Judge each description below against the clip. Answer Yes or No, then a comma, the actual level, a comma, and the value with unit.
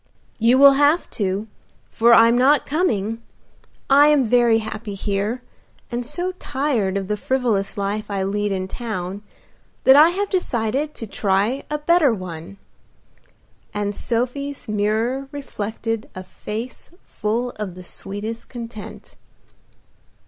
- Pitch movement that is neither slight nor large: Yes, average, 4.7 semitones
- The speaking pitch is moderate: No, high, 225 Hz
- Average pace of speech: No, slow, 130 wpm